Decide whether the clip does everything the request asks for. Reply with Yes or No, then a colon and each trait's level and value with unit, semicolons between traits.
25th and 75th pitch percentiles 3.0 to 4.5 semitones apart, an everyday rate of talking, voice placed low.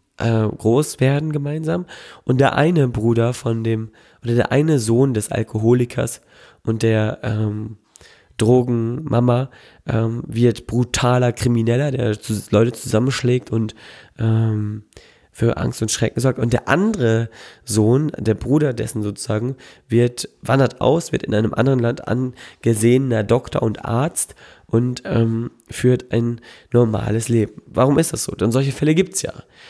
No: narrow, 2.4 semitones; average, 145 wpm; low, 120 Hz